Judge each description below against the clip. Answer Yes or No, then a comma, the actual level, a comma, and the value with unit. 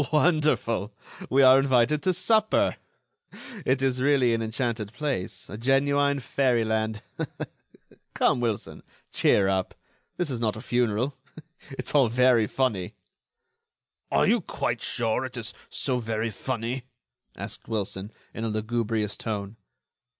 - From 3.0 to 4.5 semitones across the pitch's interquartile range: Yes, average, 3.5 semitones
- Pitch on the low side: Yes, low, 120 Hz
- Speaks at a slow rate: Yes, slow, 130 wpm